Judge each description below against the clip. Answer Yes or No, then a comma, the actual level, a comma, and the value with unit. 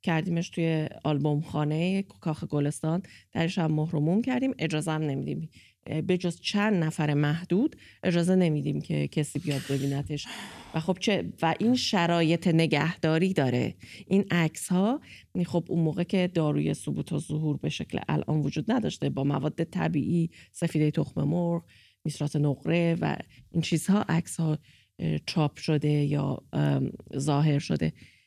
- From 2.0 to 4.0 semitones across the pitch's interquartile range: Yes, average, 2.9 semitones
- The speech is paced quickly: No, average, 140 wpm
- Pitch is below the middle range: No, medium, 160 Hz